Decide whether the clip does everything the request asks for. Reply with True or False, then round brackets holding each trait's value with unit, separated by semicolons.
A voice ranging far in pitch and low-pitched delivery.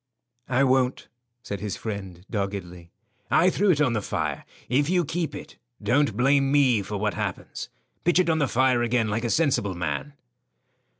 True (5.8 semitones; 125 Hz)